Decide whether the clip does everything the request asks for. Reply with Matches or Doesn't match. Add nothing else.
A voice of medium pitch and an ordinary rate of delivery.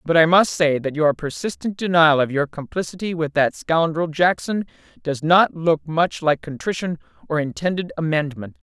Matches